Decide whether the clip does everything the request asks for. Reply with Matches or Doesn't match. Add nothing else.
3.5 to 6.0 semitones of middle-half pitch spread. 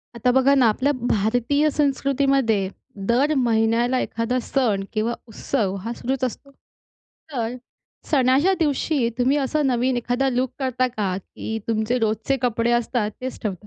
Doesn't match